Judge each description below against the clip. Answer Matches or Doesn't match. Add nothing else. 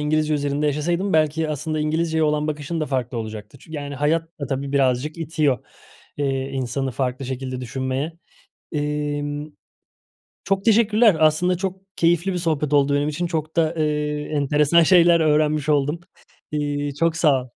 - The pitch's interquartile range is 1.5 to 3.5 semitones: Matches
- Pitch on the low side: Doesn't match